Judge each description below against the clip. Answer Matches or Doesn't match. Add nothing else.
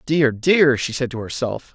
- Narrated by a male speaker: Matches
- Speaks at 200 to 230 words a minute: Matches